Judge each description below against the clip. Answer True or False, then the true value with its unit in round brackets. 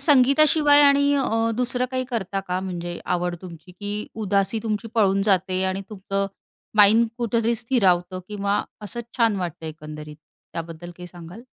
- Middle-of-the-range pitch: False (200 Hz)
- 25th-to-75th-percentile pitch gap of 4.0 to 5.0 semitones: True (4.7 semitones)